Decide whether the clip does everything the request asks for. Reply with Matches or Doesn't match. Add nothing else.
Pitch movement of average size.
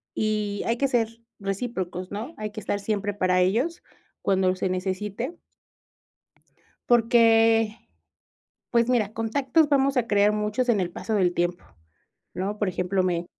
Matches